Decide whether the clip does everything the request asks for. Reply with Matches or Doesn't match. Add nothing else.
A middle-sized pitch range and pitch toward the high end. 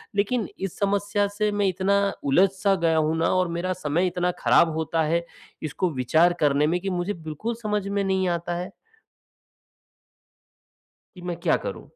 Doesn't match